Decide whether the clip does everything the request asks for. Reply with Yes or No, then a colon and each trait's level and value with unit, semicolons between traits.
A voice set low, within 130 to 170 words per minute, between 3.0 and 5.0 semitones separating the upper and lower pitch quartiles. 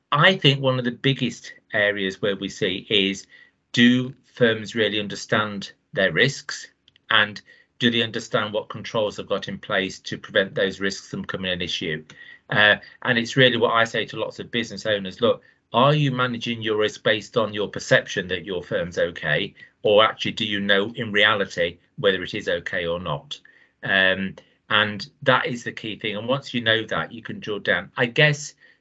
No: low, 110 Hz; average, 190 wpm; average, 3.6 semitones